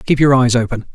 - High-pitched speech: No, low, 125 Hz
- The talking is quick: Yes, fast, 255 wpm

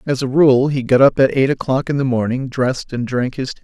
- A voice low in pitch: Yes, low, 130 Hz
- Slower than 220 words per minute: No, fast, 280 wpm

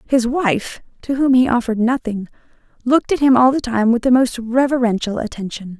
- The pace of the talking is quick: No, average, 185 wpm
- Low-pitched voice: No, high, 240 Hz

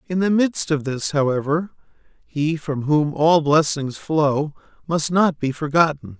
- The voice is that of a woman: No, male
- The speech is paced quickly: No, average, 155 wpm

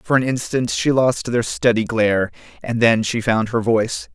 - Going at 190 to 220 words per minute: Yes, fast, 205 wpm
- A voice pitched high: No, low, 115 Hz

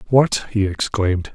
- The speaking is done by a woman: No, male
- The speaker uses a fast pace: No, slow, 135 wpm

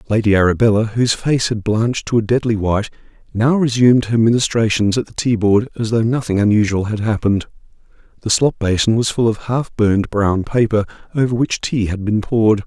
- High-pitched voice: No, low, 110 Hz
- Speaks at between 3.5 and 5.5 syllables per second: No, 5.8 syllables/s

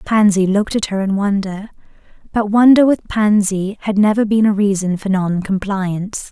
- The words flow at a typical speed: Yes, average, 170 wpm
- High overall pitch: Yes, high, 200 Hz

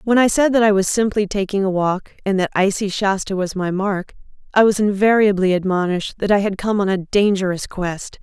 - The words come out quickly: Yes, fast, 210 wpm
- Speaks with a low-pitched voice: No, high, 195 Hz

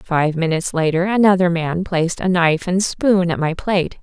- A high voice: No, medium, 175 Hz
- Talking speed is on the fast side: No, average, 195 wpm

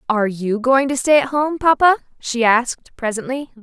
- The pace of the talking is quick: No, average, 180 wpm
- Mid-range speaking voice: No, very high, 255 Hz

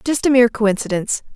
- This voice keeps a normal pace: Yes, average, 175 wpm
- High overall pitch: Yes, high, 230 Hz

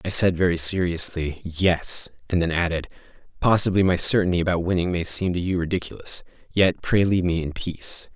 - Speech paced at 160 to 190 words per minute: Yes, average, 175 wpm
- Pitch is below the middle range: Yes, very low, 90 Hz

